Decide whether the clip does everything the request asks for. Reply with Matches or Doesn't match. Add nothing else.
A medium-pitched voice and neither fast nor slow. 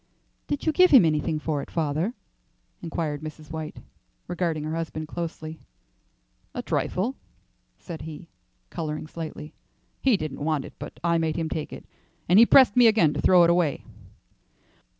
Matches